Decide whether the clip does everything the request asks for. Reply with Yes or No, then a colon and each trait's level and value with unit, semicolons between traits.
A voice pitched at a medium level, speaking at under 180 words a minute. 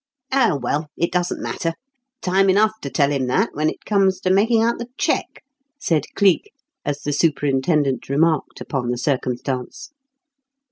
Yes: medium, 155 Hz; average, 155 wpm